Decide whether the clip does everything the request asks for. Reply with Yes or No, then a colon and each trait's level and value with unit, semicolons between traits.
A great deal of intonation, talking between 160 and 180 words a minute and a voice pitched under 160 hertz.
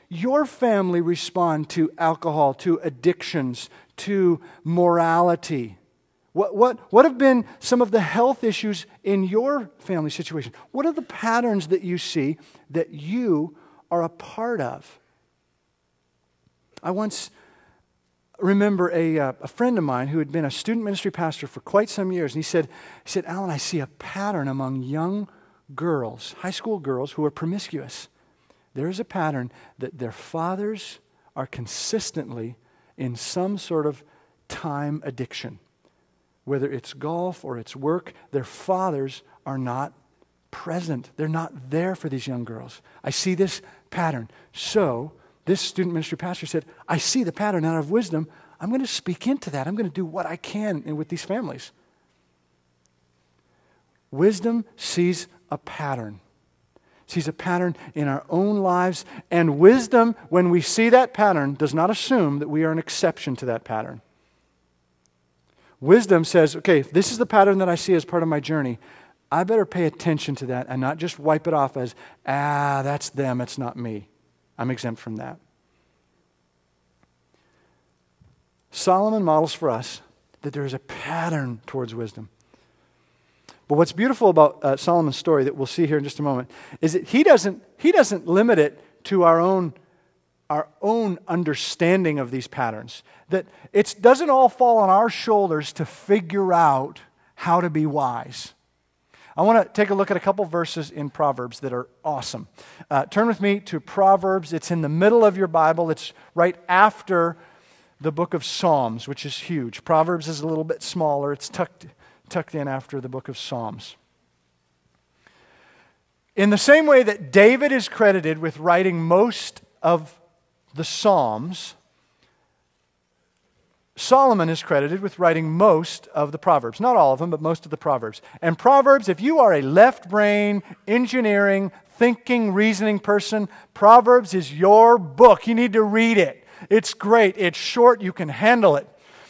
No: wide, 6.2 semitones; average, 165 wpm; medium, 165 Hz